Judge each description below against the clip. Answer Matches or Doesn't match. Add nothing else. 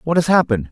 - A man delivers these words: Matches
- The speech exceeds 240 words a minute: Matches